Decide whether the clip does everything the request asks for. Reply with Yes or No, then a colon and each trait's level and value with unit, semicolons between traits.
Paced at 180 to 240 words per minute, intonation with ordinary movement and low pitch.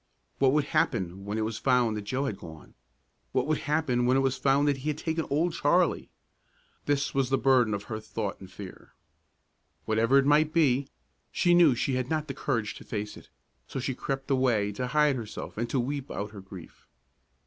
Yes: fast, 205 wpm; average, 4.7 semitones; low, 130 Hz